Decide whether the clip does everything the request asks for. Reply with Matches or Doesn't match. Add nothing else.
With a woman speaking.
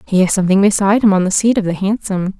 Matches